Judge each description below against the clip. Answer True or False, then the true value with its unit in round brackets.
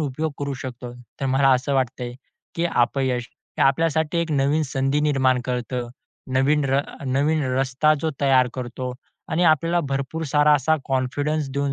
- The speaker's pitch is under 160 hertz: True (135 Hz)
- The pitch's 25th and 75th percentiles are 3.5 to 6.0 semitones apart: False (2.8 semitones)